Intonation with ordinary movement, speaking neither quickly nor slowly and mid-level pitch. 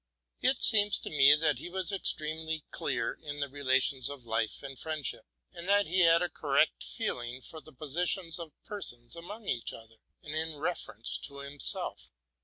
Yes: average, 4.3 semitones; average, 180 wpm; medium, 155 Hz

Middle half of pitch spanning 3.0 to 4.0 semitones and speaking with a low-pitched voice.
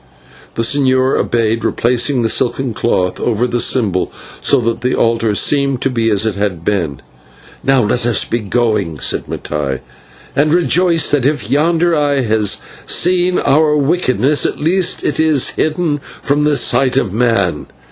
No: average, 4.9 semitones; low, 125 Hz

